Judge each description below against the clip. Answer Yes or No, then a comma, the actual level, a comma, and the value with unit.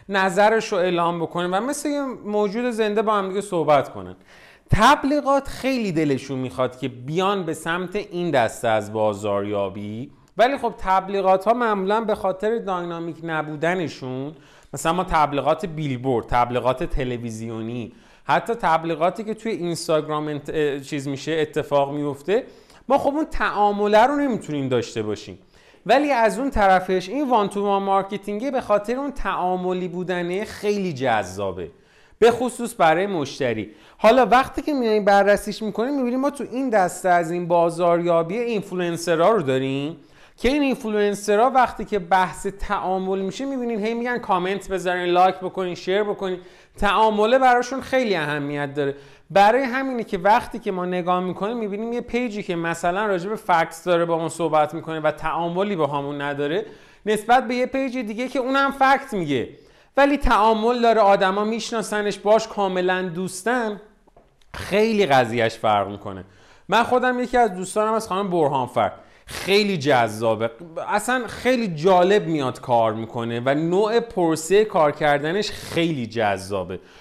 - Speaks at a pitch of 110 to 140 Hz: No, high, 190 Hz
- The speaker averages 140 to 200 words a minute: Yes, average, 145 wpm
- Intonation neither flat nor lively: No, wide, 6.2 semitones